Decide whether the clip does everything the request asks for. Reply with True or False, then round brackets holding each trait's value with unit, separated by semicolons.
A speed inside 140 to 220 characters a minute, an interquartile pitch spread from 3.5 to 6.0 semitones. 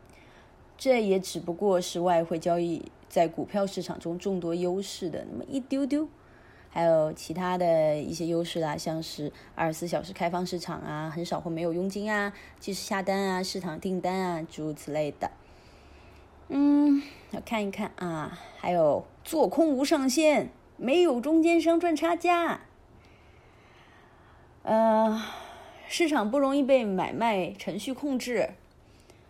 False (215 characters per minute; 8.1 semitones)